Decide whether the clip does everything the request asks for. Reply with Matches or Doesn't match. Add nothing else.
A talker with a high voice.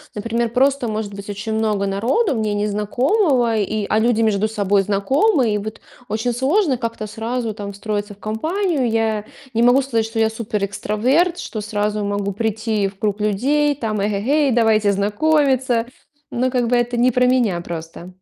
Matches